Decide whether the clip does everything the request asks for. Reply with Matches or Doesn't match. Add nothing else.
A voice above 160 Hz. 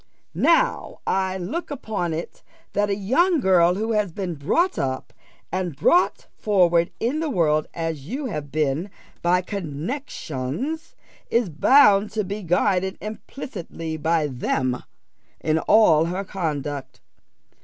Matches